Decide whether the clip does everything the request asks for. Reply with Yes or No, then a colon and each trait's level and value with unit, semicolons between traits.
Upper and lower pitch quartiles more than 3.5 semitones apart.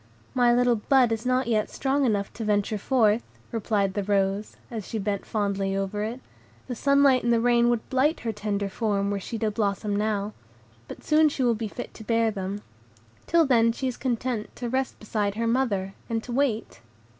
No: average, 3.2 semitones